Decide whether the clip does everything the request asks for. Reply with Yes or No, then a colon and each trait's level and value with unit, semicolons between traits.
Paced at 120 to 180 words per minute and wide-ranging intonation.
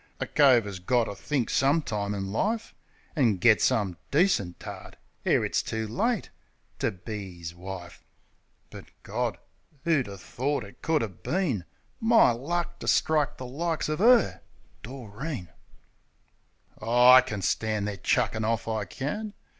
Yes: average, 155 wpm; wide, 7.1 semitones